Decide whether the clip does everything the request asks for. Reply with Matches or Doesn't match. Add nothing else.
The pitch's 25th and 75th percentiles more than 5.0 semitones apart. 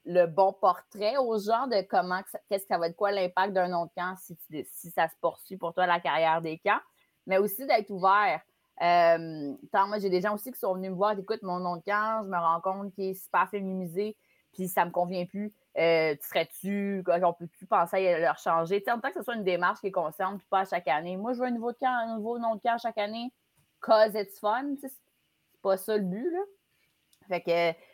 Doesn't match